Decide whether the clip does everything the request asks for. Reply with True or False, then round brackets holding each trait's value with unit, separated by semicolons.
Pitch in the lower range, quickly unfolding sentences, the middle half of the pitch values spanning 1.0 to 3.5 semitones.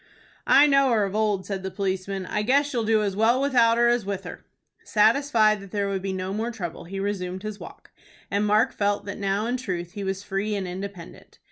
False (205 Hz; 225 wpm; 2.7 semitones)